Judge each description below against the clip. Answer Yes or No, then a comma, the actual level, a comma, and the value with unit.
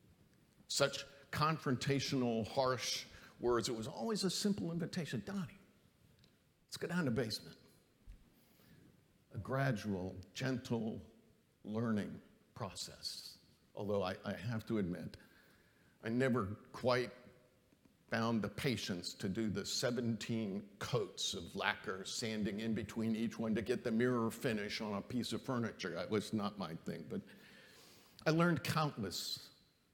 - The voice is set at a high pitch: No, low, 120 Hz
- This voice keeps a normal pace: No, slow, 130 wpm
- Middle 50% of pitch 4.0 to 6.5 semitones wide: No, average, 3.5 semitones